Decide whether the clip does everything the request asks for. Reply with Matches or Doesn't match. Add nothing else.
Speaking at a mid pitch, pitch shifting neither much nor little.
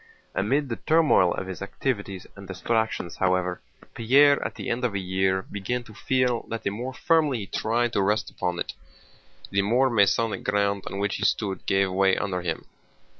Doesn't match